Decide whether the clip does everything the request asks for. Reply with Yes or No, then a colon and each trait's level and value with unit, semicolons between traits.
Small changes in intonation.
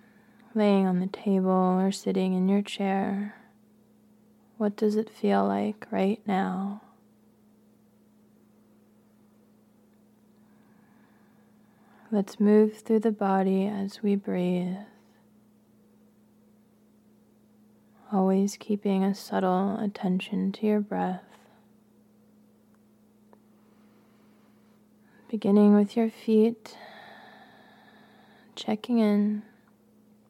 Yes: narrow, 1.1 semitones